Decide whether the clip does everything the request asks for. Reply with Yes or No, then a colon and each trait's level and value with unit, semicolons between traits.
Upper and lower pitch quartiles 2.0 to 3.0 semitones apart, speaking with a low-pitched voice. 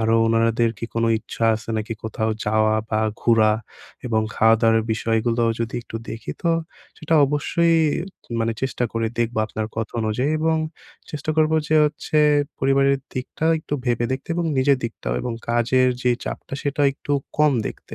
No: average, 3.8 semitones; low, 120 Hz